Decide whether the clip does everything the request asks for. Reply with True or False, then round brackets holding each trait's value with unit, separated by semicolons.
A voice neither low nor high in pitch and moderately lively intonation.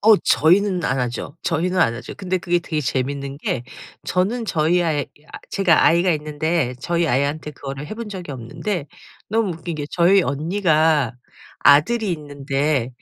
True (160 Hz; 4.4 semitones)